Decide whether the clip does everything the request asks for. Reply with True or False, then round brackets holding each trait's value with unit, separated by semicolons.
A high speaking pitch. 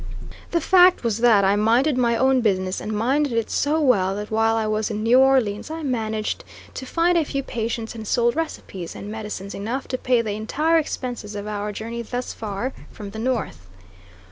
True (230 Hz)